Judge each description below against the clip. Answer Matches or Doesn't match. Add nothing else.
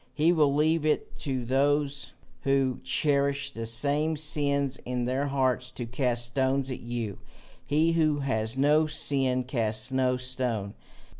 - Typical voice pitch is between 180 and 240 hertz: Doesn't match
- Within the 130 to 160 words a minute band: Matches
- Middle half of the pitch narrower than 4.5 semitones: Matches